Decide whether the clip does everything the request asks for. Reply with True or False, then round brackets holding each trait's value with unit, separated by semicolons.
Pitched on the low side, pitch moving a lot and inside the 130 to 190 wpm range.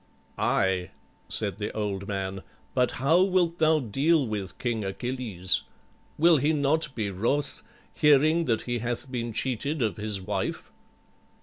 True (120 Hz; 6.4 semitones; 145 wpm)